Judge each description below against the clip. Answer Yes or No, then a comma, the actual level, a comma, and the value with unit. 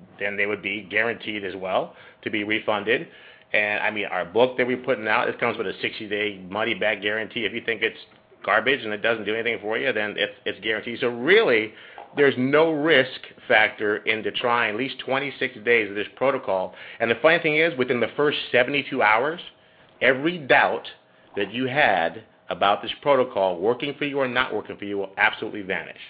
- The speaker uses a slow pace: No, average, 200 wpm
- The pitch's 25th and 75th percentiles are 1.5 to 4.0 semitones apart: No, average, 5.0 semitones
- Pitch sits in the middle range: No, low, 120 Hz